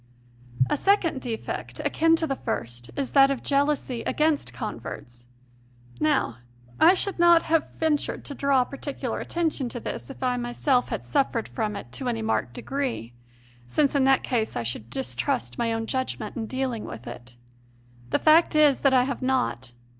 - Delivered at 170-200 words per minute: Yes, average, 175 wpm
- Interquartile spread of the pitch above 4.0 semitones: Yes, average, 4.9 semitones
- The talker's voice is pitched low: No, very high, 260 Hz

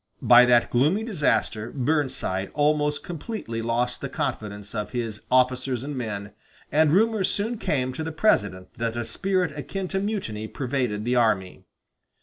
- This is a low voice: Yes, low, 125 Hz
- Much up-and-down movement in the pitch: Yes, wide, 5.7 semitones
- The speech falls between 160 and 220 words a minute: No, average, 150 wpm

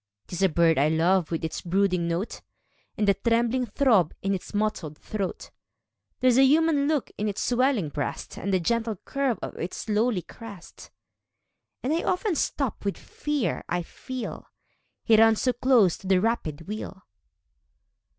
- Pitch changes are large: Yes, wide, 5.7 semitones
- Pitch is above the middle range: Yes, high, 210 Hz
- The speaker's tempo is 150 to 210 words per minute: Yes, average, 170 wpm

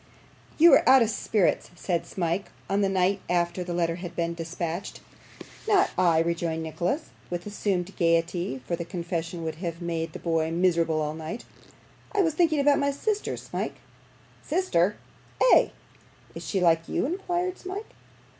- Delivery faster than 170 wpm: No, average, 160 wpm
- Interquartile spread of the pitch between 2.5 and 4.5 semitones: No, wide, 5.5 semitones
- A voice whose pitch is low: No, medium, 175 Hz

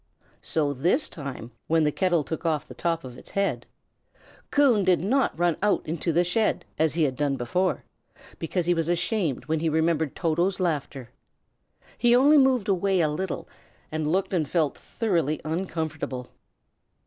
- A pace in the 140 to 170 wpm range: Yes, average, 165 wpm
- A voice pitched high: No, medium, 165 Hz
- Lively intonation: No, average, 3.7 semitones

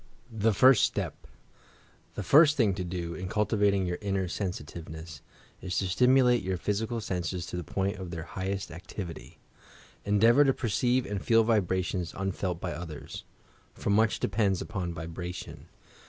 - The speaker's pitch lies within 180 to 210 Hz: No, very low, 95 Hz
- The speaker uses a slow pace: No, average, 155 wpm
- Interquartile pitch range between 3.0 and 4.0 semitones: Yes, average, 3.6 semitones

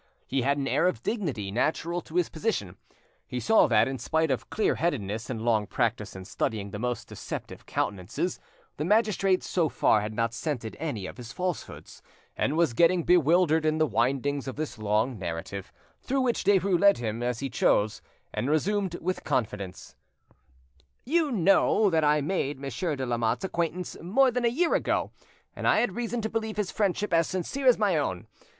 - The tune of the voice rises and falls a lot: Yes, wide, 8.2 semitones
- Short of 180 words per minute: No, average, 185 wpm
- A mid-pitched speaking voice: Yes, medium, 155 Hz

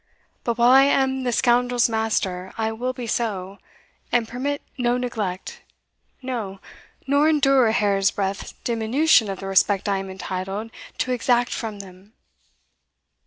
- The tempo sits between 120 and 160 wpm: Yes, average, 145 wpm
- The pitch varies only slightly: No, average, 4.1 semitones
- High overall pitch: Yes, high, 225 Hz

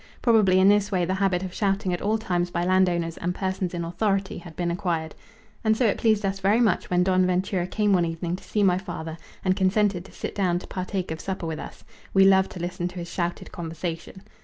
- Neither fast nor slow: No, fast, 235 wpm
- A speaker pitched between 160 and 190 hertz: Yes, medium, 185 Hz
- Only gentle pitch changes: Yes, narrow, 2.0 semitones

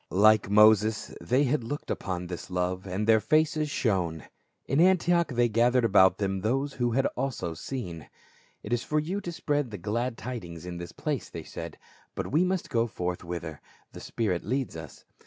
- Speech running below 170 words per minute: No, average, 190 wpm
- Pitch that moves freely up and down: Yes, wide, 6.8 semitones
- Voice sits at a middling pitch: No, low, 110 Hz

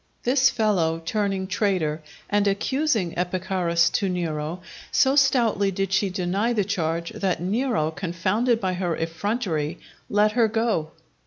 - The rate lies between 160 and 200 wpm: No, slow, 135 wpm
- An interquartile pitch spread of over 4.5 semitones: No, average, 4.2 semitones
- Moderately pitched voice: No, high, 195 Hz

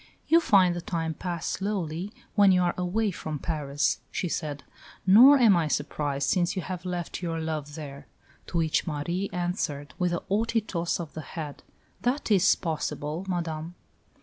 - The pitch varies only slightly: No, average, 3.4 semitones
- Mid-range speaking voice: Yes, medium, 175 Hz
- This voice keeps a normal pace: Yes, average, 170 wpm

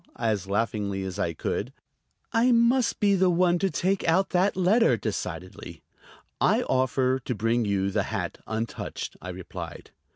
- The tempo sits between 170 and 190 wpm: No, average, 155 wpm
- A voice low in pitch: Yes, low, 130 Hz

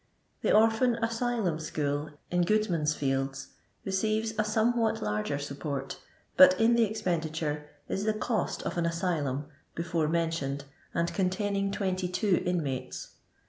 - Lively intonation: Yes, wide, 6.3 semitones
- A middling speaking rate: No, slow, 125 wpm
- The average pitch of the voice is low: No, medium, 175 Hz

